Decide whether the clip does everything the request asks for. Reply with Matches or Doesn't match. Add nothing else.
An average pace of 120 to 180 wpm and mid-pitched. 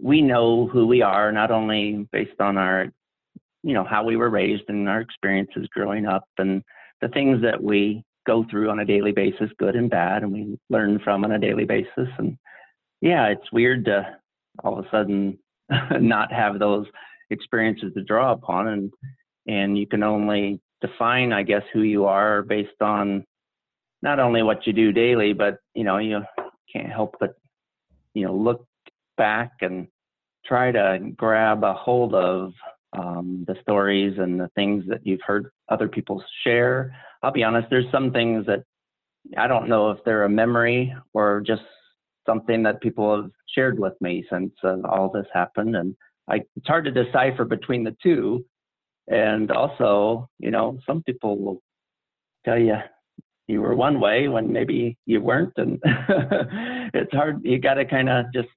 Doesn't match